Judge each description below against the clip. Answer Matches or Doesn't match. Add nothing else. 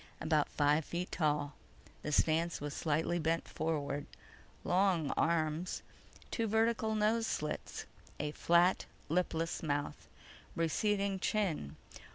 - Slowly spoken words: Matches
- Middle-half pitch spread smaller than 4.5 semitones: Matches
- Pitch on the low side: Doesn't match